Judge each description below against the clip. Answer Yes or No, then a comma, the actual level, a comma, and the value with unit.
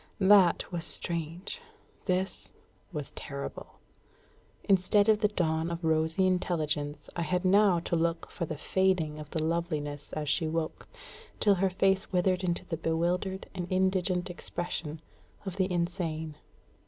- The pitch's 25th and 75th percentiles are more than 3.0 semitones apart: No, average, 2.7 semitones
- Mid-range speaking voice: Yes, medium, 175 Hz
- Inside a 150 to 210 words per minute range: No, average, 140 wpm